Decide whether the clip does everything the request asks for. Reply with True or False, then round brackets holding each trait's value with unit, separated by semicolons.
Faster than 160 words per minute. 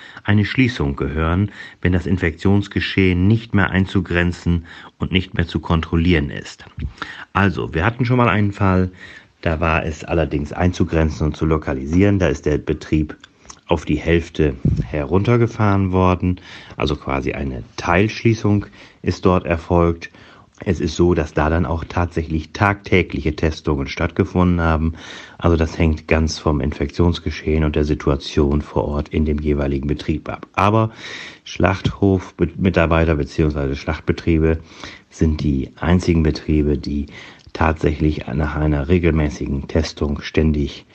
False (130 wpm)